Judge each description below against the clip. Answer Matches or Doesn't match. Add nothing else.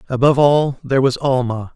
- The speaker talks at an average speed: Matches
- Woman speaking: Doesn't match